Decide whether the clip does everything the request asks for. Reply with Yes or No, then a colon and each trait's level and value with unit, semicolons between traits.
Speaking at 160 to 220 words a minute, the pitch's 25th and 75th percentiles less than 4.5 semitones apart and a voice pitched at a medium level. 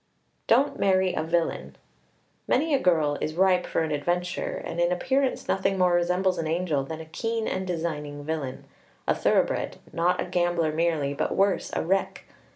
Yes: average, 170 wpm; average, 2.9 semitones; medium, 175 Hz